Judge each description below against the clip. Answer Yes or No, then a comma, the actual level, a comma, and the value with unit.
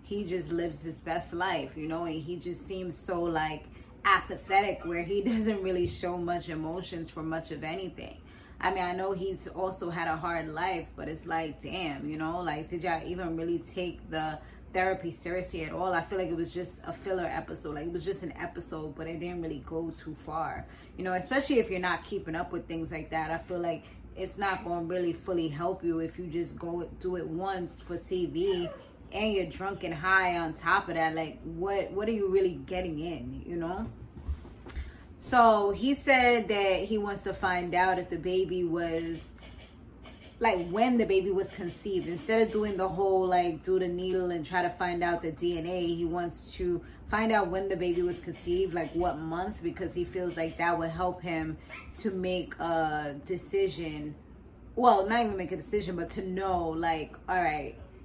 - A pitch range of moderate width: No, narrow, 2.2 semitones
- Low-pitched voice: No, medium, 175 Hz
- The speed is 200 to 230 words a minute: Yes, fast, 205 wpm